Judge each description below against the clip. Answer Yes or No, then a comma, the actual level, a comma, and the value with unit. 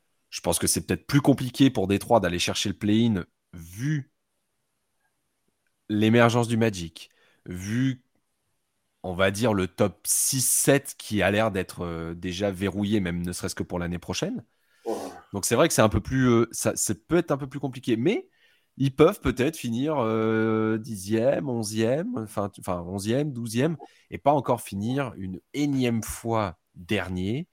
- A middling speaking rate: Yes, average, 160 wpm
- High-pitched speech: No, low, 110 Hz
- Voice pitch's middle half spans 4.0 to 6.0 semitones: Yes, average, 4.8 semitones